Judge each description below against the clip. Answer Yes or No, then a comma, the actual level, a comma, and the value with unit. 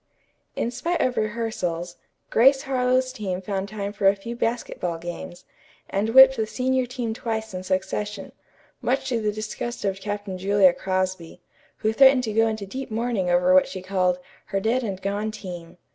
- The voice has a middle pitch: No, high, 210 Hz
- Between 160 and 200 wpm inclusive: Yes, average, 175 wpm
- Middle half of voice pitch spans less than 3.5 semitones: No, average, 4.1 semitones